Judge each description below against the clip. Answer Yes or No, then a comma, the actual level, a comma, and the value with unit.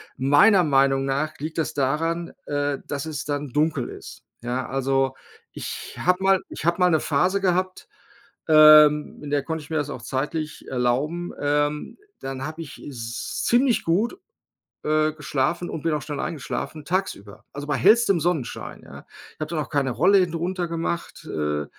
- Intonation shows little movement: No, average, 3.7 semitones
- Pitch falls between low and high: Yes, medium, 150 Hz